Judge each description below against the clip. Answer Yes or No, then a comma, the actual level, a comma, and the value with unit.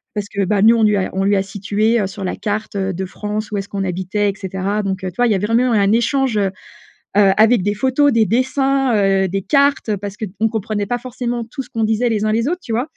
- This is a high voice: Yes, high, 210 Hz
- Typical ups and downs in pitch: Yes, average, 3.1 semitones